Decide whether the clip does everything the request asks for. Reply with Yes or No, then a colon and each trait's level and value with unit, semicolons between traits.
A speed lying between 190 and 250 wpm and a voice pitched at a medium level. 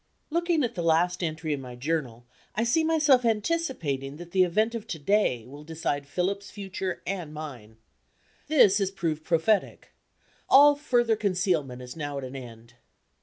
No: average, 165 wpm; medium, 175 Hz